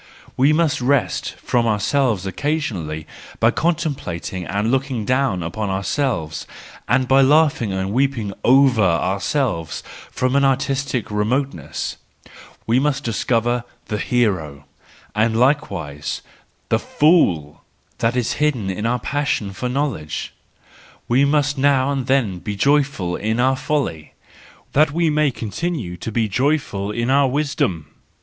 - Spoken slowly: Yes, slow, 130 wpm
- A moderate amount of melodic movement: No, wide, 6.1 semitones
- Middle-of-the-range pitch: No, low, 125 Hz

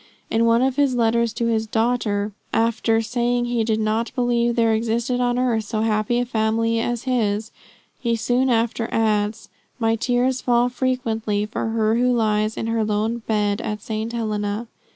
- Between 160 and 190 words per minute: Yes, average, 175 wpm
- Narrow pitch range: Yes, narrow, 1.8 semitones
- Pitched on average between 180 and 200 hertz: No, high, 230 Hz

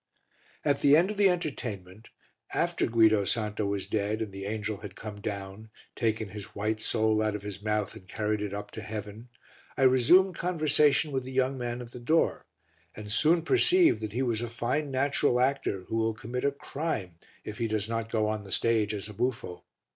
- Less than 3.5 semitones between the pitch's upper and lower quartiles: No, average, 3.9 semitones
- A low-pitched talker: Yes, low, 110 Hz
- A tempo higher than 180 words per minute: Yes, average, 200 wpm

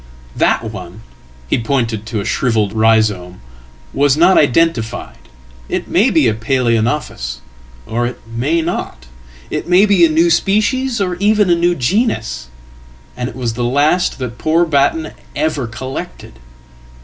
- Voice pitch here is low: Yes, low, 130 Hz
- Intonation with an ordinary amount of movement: No, wide, 7.1 semitones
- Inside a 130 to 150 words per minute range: Yes, average, 140 wpm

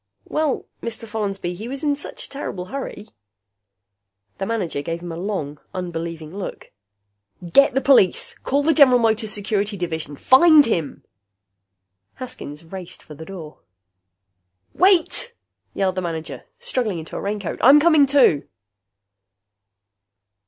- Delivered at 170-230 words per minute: No, slow, 135 wpm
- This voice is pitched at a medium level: No, high, 200 Hz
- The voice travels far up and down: Yes, wide, 8.3 semitones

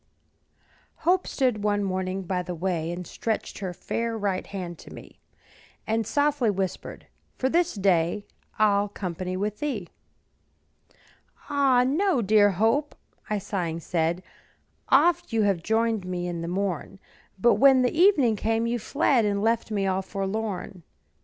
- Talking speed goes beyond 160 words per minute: No, average, 145 wpm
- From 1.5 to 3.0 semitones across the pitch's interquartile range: No, average, 4.4 semitones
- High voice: Yes, high, 205 Hz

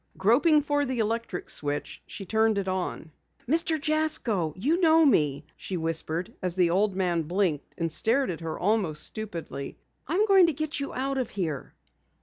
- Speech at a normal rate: Yes, average, 170 wpm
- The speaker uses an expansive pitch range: Yes, wide, 8.9 semitones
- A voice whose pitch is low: No, high, 210 Hz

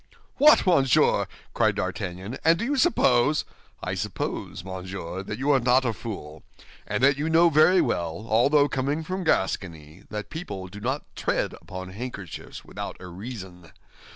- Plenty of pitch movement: Yes, wide, 8.0 semitones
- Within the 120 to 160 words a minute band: Yes, average, 155 wpm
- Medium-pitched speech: No, low, 120 Hz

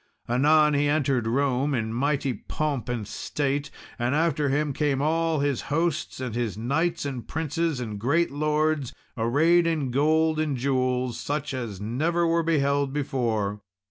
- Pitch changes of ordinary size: Yes, average, 3.7 semitones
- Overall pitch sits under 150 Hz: Yes, medium, 140 Hz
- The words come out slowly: No, average, 150 wpm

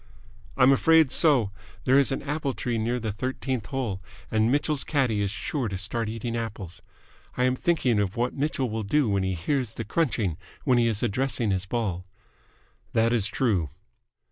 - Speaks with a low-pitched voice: Yes, low, 115 Hz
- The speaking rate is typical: Yes, average, 180 wpm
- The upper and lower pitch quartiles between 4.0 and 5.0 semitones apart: Yes, average, 4.4 semitones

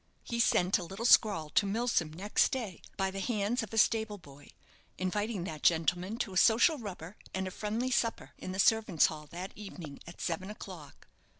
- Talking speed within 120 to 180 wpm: No, average, 190 wpm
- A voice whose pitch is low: No, high, 195 Hz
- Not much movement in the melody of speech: No, average, 4.1 semitones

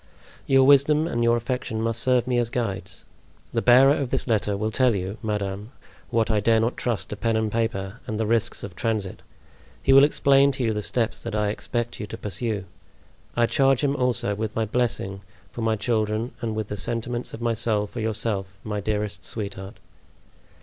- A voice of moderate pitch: No, low, 115 Hz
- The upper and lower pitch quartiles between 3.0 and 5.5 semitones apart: No, narrow, 2.5 semitones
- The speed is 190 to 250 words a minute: Yes, average, 200 wpm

